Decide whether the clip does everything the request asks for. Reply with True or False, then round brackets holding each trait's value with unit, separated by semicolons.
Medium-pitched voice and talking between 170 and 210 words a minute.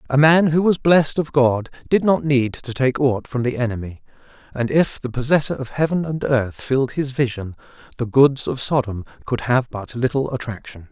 False (130 Hz; 200 wpm)